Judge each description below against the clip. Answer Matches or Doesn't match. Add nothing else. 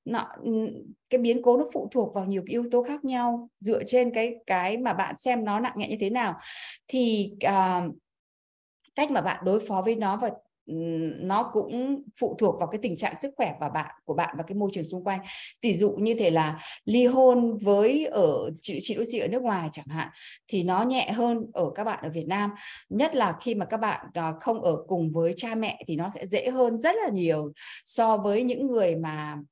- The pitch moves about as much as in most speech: Matches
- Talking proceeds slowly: Doesn't match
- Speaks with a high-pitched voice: Matches